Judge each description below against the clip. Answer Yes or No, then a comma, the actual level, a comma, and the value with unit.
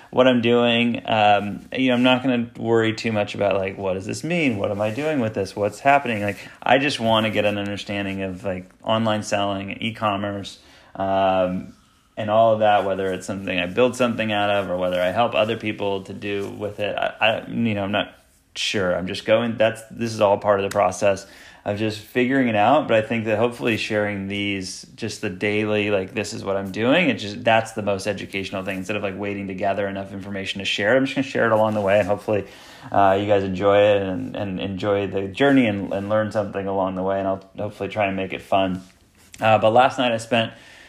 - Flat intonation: Yes, narrow, 2.2 semitones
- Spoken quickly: Yes, fast, 235 wpm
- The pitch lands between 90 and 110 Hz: Yes, low, 105 Hz